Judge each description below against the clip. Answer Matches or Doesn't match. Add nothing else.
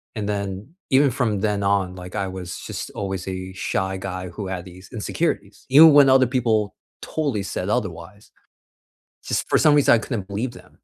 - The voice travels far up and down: Doesn't match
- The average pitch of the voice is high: Doesn't match